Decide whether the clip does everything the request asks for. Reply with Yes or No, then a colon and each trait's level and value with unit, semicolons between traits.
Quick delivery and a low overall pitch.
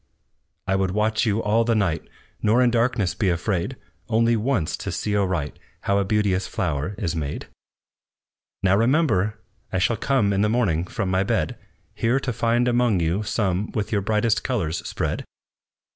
No: average, 170 wpm; low, 105 Hz